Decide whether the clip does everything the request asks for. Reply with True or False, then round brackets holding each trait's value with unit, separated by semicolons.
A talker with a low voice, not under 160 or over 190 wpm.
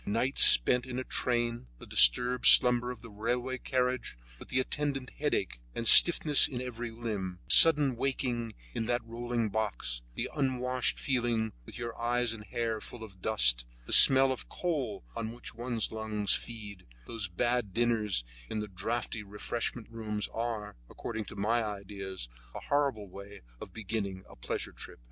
True (115 Hz; 165 wpm)